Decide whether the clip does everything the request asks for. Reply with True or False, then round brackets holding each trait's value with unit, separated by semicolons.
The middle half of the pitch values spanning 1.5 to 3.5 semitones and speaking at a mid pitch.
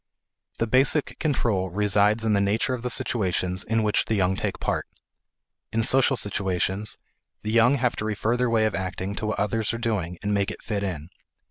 False (2.9 semitones; 105 Hz)